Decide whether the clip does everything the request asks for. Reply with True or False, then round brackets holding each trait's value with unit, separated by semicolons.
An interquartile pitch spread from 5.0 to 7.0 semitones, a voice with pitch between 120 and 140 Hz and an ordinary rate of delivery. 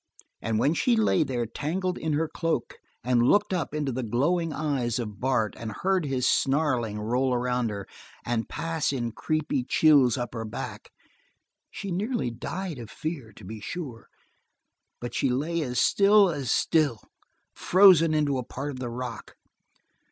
True (5.4 semitones; 135 Hz; 165 wpm)